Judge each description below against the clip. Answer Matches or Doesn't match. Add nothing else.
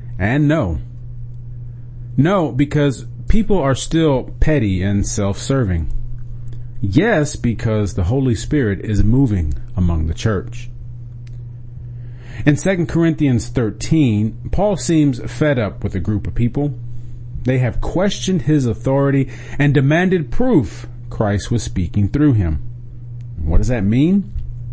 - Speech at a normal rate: Doesn't match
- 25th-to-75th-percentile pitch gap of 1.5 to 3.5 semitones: Doesn't match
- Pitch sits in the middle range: Doesn't match